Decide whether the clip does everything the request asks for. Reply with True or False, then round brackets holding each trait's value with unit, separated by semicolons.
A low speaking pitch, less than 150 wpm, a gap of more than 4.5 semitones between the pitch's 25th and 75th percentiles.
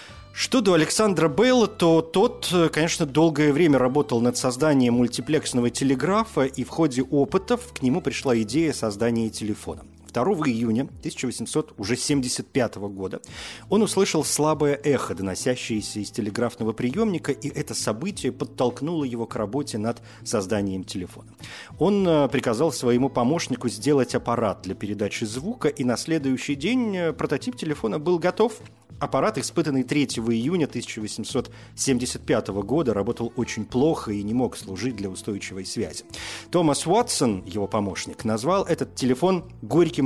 True (130 Hz; 130 wpm; 5.3 semitones)